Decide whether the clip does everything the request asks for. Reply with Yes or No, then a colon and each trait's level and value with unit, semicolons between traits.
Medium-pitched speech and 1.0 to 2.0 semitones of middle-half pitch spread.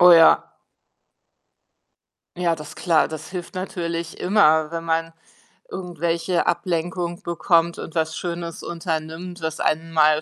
Yes: medium, 170 Hz; narrow, 1.4 semitones